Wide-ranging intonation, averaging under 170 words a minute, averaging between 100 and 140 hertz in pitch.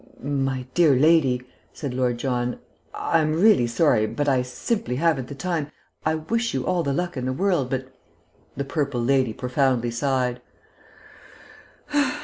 No: average, 3.9 semitones; average, 150 wpm; low, 135 Hz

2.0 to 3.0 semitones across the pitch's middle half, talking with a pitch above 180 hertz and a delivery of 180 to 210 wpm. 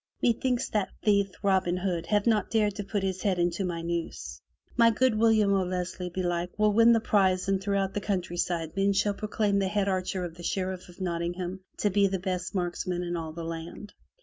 Yes: narrow, 2.6 semitones; high, 190 Hz; average, 200 wpm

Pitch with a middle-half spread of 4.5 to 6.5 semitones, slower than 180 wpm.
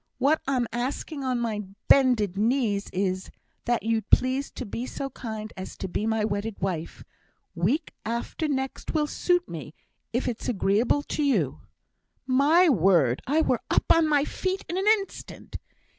Yes: wide, 5.6 semitones; average, 160 wpm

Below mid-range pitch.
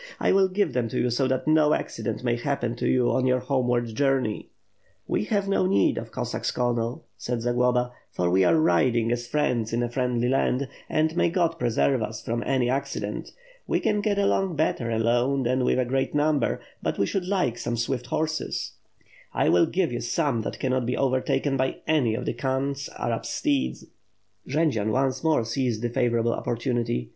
Yes: low, 125 Hz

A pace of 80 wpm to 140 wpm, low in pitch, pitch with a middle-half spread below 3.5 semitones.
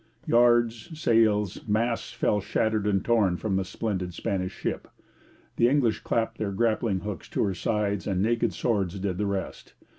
No: average, 160 wpm; low, 105 Hz; average, 3.0 semitones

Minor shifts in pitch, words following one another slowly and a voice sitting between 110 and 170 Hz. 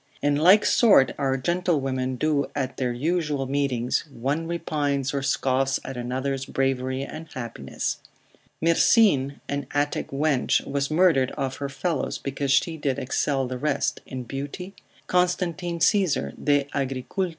No: average, 3.2 semitones; slow, 130 wpm; medium, 140 Hz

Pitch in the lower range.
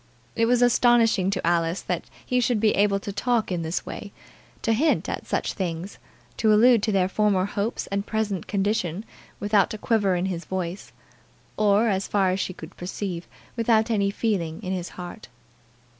No: high, 200 Hz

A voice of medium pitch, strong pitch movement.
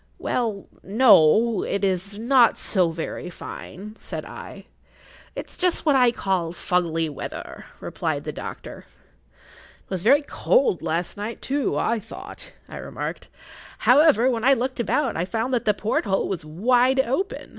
No: high, 225 Hz; wide, 5.8 semitones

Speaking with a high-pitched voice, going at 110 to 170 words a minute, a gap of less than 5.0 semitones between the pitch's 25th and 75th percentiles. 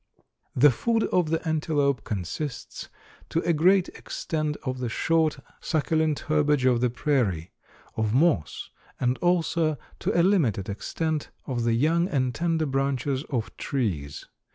No: medium, 145 Hz; average, 140 wpm; average, 4.5 semitones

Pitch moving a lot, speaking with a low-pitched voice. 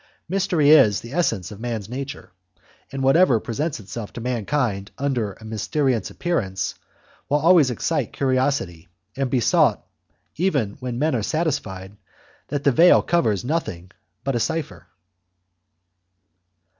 Yes: wide, 5.7 semitones; low, 130 Hz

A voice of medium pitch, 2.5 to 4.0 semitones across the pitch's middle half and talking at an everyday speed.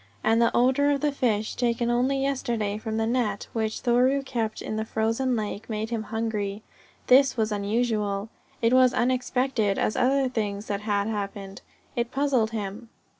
No: high, 225 Hz; average, 3.0 semitones; average, 170 wpm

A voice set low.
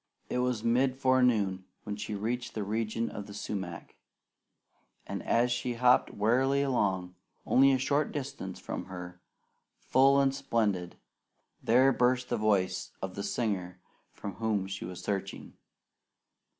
Yes: low, 110 Hz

